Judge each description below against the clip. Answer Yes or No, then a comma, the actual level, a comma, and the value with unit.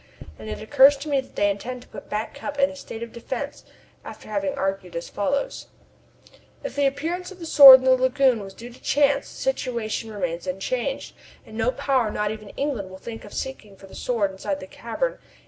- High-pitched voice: Yes, high, 240 Hz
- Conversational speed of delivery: No, fast, 215 wpm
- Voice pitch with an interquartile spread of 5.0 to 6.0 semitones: Yes, wide, 5.4 semitones